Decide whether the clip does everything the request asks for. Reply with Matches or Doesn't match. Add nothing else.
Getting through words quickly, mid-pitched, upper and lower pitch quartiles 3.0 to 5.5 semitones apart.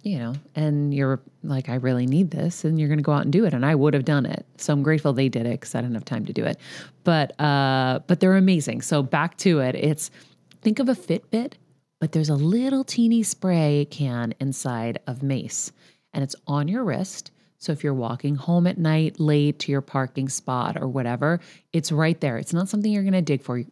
Matches